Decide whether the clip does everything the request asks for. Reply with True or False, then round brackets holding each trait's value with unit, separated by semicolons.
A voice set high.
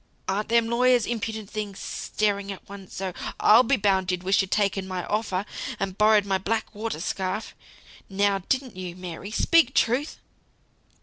True (205 Hz)